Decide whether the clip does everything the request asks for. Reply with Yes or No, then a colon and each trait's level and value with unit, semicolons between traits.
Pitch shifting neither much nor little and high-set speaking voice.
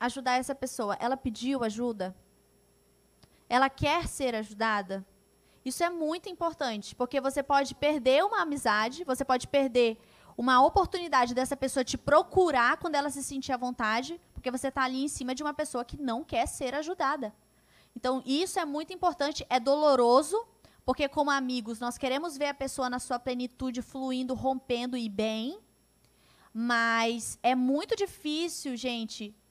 Yes: average, 3.0 semitones; very high, 260 Hz